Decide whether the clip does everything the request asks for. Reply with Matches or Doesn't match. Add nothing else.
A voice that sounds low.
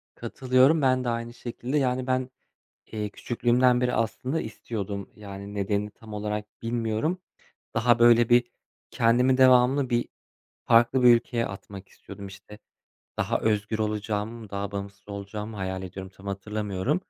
Matches